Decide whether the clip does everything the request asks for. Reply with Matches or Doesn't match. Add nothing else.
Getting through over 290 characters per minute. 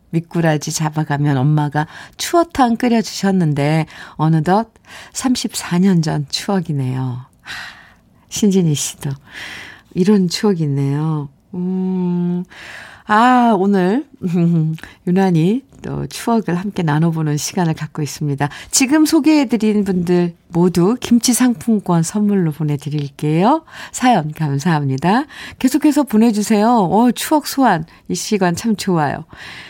Doesn't match